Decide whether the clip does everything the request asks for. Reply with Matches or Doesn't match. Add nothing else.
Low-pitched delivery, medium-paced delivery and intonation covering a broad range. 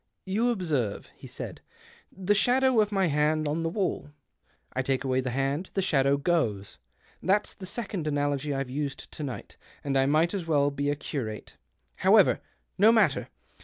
Doesn't match